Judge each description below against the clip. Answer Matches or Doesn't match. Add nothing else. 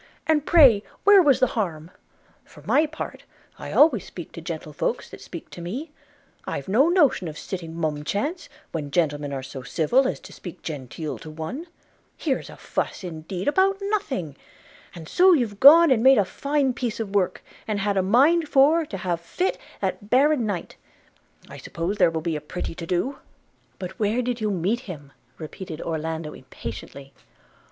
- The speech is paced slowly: Doesn't match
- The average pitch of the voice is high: Matches